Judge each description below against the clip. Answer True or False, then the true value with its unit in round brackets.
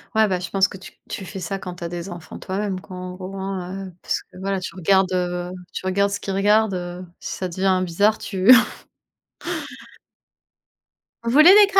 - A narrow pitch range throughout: True (1.6 semitones)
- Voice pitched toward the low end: False (190 Hz)